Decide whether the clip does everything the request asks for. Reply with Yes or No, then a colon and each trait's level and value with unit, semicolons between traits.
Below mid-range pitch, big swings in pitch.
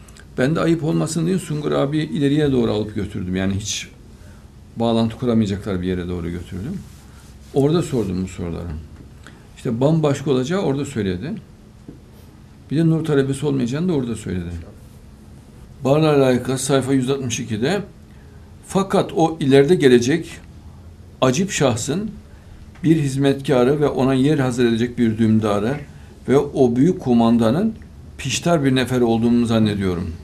Yes: low, 120 Hz; wide, 6.4 semitones